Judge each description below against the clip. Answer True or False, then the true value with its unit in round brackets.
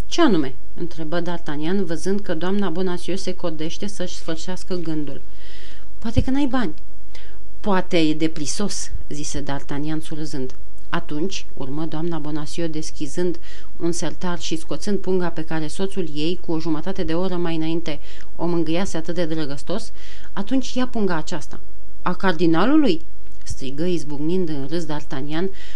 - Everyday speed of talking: True (140 wpm)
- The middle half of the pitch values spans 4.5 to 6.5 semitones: False (2.9 semitones)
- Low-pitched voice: False (170 Hz)